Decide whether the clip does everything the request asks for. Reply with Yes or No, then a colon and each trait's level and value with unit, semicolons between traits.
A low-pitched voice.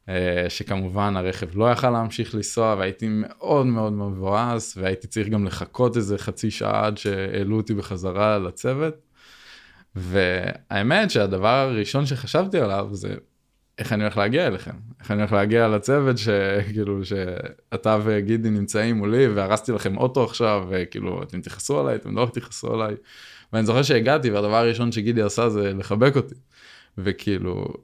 Yes: low, 105 Hz